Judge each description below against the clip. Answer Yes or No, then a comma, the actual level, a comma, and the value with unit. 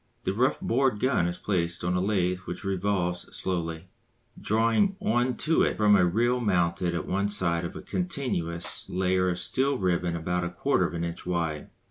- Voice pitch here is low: Yes, very low, 90 Hz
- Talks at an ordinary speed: Yes, average, 180 wpm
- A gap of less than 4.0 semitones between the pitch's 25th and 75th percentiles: No, average, 4.3 semitones